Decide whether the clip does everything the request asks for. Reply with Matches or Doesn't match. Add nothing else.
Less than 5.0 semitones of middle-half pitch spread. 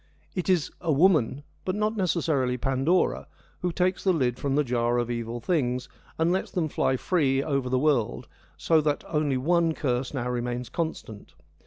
Doesn't match